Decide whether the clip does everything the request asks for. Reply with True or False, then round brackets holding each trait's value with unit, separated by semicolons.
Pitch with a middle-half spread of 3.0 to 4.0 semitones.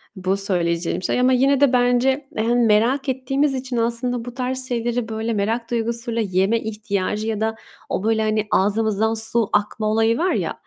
False (2.5 semitones)